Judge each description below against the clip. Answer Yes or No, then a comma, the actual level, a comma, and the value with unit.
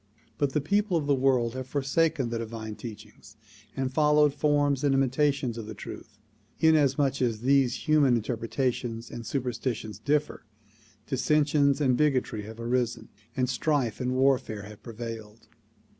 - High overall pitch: No, low, 130 Hz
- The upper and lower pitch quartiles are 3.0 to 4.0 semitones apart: Yes, average, 3.7 semitones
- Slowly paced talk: No, average, 145 wpm